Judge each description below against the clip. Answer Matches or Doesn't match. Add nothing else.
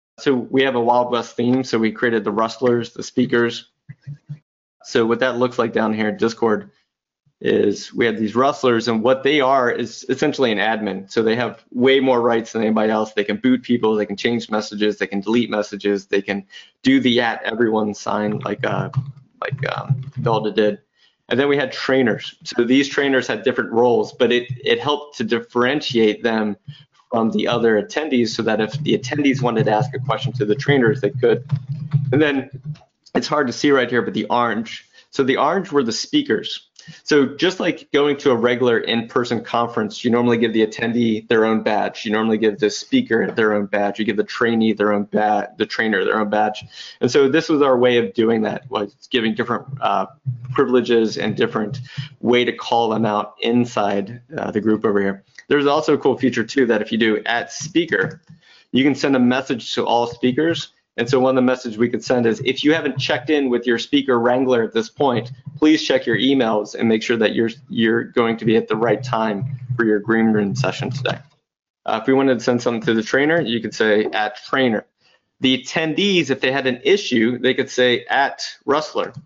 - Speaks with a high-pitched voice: Doesn't match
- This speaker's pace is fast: Matches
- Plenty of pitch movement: Doesn't match